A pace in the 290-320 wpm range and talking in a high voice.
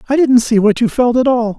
Yes: fast, 305 wpm; high, 240 Hz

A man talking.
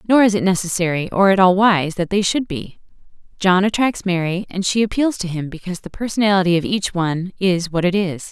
No: female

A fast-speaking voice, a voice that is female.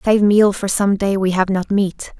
Yes: fast, 245 wpm; female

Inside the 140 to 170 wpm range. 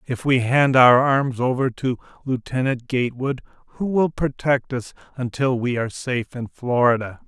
Yes: average, 155 wpm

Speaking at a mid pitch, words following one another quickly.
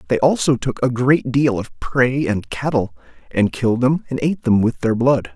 No: low, 125 Hz; fast, 215 wpm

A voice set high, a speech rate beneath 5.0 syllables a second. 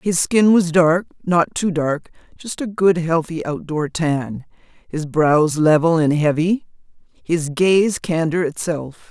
No: medium, 165 Hz; 3.6 syllables/s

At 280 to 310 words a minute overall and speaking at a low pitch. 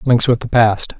No: fast, 240 wpm; low, 120 Hz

